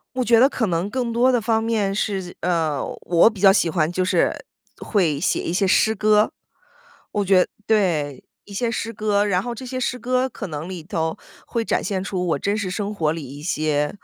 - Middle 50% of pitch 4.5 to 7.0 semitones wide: Yes, average, 4.9 semitones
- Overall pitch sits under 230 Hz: Yes, high, 200 Hz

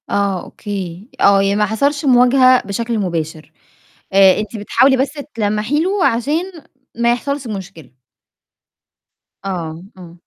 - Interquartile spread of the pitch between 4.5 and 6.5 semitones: Yes, average, 5.1 semitones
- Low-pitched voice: No, high, 210 Hz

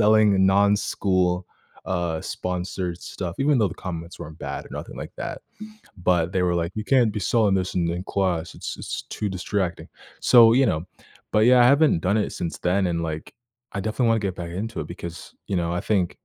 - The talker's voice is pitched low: Yes, very low, 95 Hz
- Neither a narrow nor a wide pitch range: Yes, average, 3.6 semitones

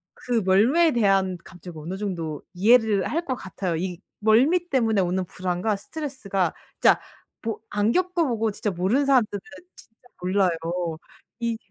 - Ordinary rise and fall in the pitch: Yes, average, 4.8 semitones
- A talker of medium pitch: No, high, 210 Hz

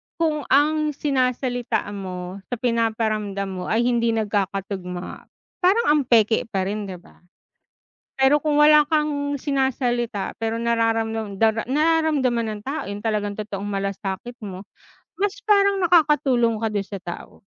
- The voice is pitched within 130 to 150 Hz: No, high, 230 Hz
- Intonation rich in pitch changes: Yes, wide, 5.9 semitones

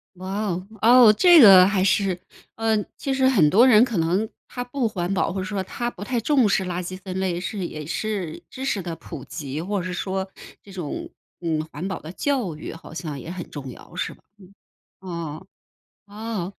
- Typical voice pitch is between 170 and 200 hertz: Yes, high, 190 Hz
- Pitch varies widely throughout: No, average, 4.0 semitones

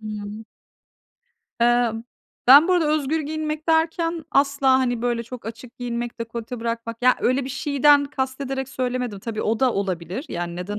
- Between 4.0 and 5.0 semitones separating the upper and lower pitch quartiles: No, average, 3.6 semitones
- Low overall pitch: No, very high, 250 Hz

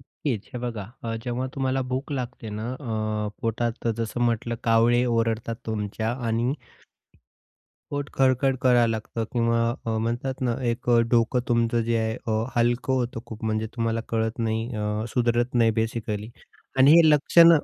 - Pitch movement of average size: No, narrow, 1.9 semitones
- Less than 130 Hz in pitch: Yes, low, 115 Hz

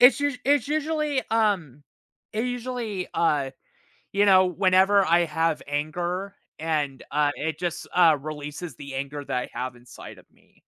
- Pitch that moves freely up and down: Yes, wide, 6.3 semitones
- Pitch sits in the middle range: Yes, medium, 175 Hz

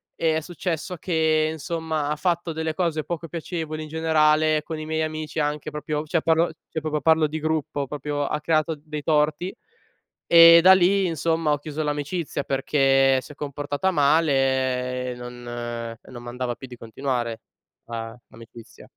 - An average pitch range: Yes, average, 3.1 semitones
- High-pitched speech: No, medium, 150 Hz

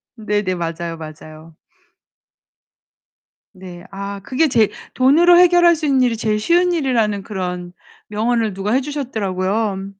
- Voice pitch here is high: Yes, high, 215 Hz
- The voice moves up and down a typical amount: No, wide, 5.8 semitones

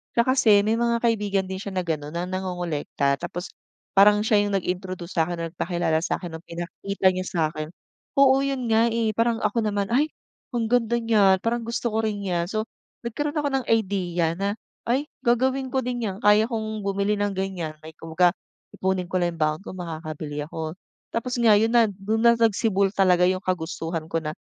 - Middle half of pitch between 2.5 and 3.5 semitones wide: No, average, 4.7 semitones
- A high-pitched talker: Yes, high, 195 Hz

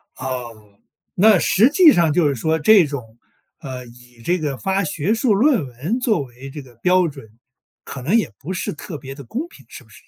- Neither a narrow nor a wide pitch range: No, wide, 7.0 semitones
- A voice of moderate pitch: Yes, medium, 155 Hz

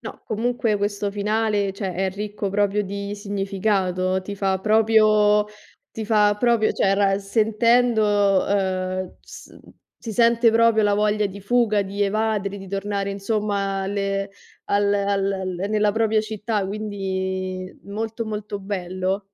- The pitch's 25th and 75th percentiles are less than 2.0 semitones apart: Yes, narrow, 1.5 semitones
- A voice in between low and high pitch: No, high, 205 Hz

